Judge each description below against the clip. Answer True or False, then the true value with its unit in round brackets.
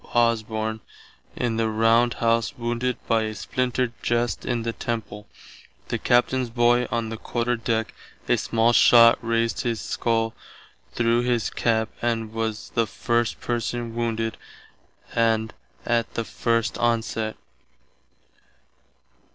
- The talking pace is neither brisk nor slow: False (125 wpm)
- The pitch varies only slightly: True (1.0 semitones)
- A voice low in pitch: True (115 Hz)